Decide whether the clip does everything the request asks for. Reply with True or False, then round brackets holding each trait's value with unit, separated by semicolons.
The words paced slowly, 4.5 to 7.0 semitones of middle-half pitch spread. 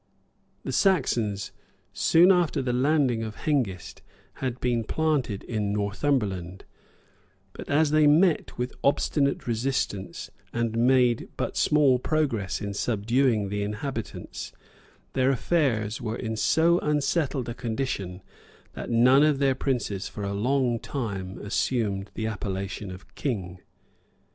True (130 wpm; 5.2 semitones)